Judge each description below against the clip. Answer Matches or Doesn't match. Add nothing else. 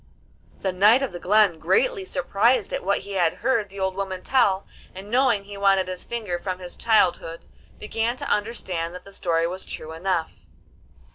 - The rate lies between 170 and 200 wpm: Matches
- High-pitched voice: Matches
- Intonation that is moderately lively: Matches